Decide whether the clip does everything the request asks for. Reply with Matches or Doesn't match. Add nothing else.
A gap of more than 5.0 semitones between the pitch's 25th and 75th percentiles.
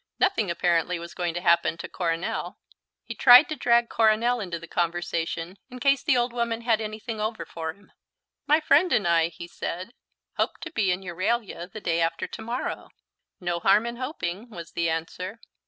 Matches